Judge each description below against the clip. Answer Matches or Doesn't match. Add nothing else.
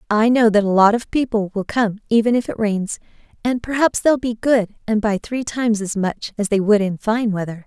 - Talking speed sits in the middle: Doesn't match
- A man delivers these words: Doesn't match